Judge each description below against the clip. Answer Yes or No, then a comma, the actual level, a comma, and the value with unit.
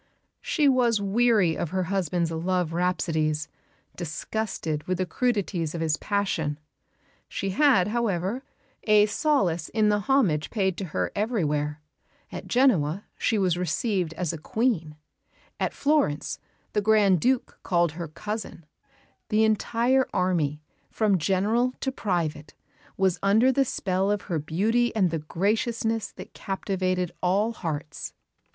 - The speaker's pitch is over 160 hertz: Yes, high, 190 Hz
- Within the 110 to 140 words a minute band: Yes, slow, 135 wpm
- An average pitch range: Yes, average, 4.9 semitones